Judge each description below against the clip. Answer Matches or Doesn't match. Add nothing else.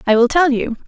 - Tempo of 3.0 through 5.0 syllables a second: Doesn't match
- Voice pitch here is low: Doesn't match